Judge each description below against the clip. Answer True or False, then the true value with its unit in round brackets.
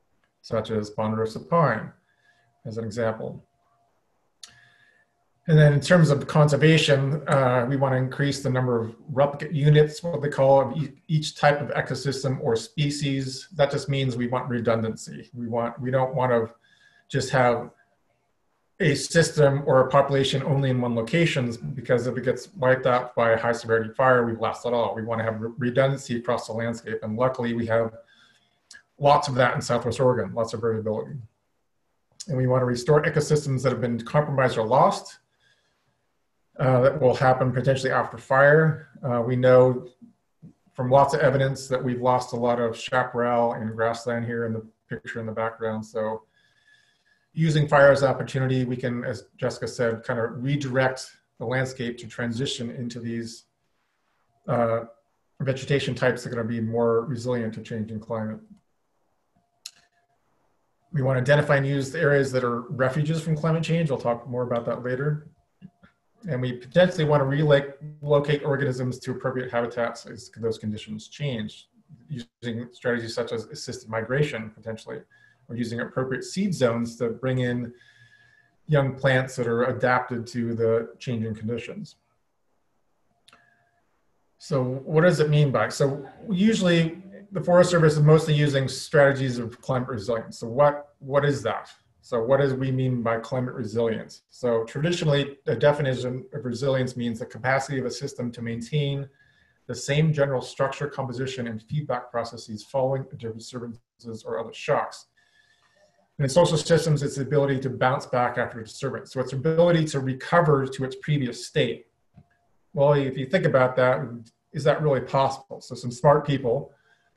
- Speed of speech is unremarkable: True (160 wpm)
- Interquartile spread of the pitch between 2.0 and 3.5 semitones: True (3.2 semitones)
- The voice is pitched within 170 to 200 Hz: False (130 Hz)